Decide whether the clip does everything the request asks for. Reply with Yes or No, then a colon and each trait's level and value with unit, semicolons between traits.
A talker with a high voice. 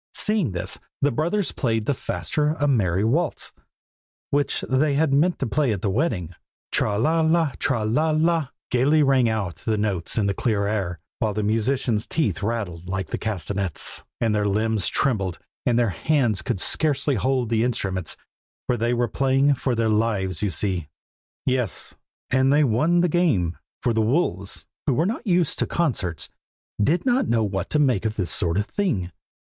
No: low, 115 Hz